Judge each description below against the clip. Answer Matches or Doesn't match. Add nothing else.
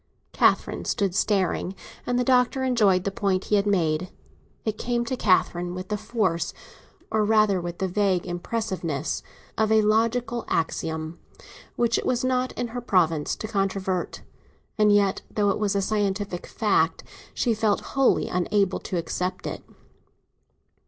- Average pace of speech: Matches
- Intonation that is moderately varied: Matches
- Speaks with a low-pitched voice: Doesn't match